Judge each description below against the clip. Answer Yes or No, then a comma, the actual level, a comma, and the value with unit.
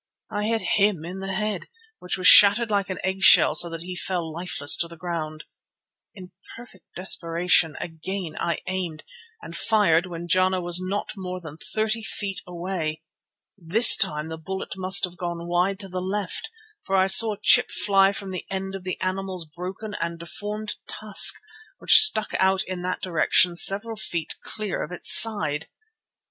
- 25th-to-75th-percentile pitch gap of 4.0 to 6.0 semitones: No, narrow, 2.5 semitones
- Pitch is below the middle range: No, medium, 185 Hz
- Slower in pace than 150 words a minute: No, average, 175 wpm